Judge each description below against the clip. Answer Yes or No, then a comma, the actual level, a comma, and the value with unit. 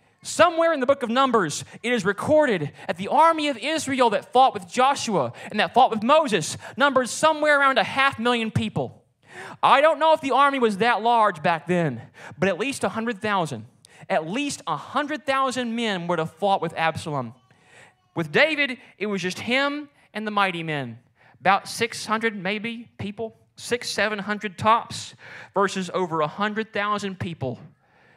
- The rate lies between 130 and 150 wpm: No, average, 160 wpm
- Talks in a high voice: Yes, high, 210 Hz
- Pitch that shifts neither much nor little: No, wide, 7.5 semitones